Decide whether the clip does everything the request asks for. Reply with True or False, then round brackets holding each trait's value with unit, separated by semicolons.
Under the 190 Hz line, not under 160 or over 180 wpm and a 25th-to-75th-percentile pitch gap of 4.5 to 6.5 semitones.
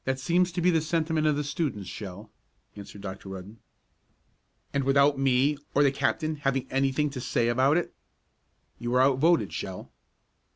False (135 Hz; 170 wpm; 4.1 semitones)